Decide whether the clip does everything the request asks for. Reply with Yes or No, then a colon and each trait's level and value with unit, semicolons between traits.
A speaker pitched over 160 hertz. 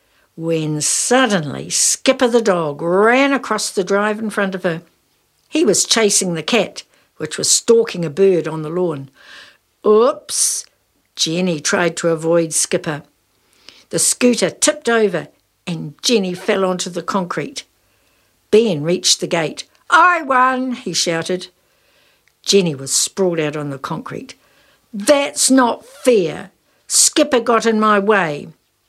Yes: high, 190 Hz